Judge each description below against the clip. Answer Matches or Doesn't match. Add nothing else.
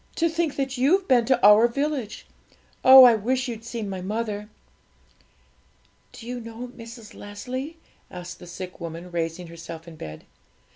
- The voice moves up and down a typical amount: Doesn't match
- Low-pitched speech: Doesn't match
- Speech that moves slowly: Doesn't match